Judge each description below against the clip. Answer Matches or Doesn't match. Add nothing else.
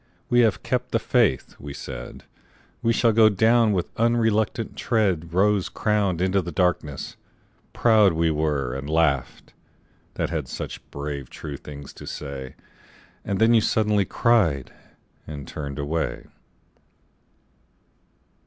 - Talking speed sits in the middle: Doesn't match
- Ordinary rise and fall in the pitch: Doesn't match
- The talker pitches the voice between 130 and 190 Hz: Doesn't match